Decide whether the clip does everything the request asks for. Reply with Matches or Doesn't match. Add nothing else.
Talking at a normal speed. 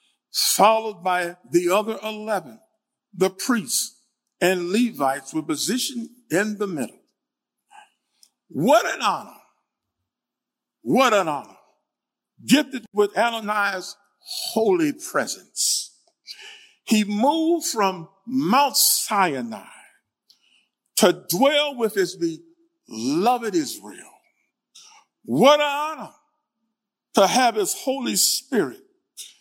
Doesn't match